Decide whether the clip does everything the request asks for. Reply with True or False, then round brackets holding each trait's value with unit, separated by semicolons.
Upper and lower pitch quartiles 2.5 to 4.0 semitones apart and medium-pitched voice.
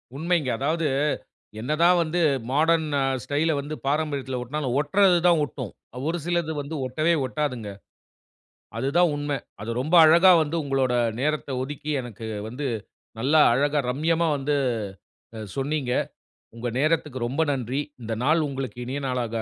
True (3.5 semitones; 145 Hz)